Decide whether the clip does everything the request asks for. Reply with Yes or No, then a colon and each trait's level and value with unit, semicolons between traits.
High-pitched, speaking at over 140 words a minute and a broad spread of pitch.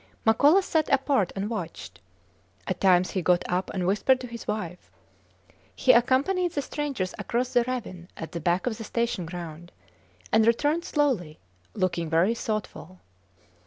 Yes: high, 215 Hz; average, 155 wpm; wide, 6.3 semitones